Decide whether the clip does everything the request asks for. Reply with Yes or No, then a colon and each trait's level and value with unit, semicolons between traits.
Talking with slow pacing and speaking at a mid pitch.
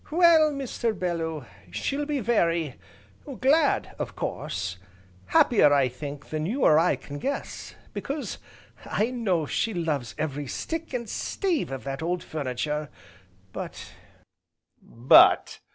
Yes: slow, 130 wpm; medium, 170 Hz